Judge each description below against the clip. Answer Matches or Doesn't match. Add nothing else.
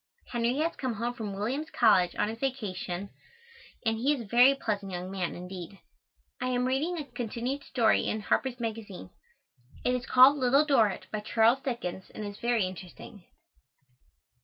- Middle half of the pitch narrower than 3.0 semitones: Doesn't match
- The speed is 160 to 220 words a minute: Matches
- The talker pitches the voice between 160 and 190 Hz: Doesn't match